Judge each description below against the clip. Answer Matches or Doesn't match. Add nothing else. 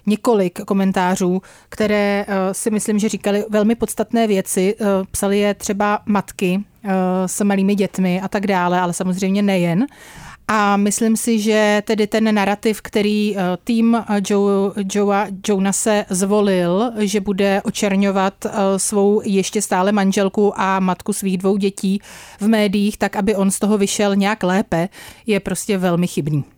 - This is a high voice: Matches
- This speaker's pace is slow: Doesn't match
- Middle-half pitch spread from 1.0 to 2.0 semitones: Matches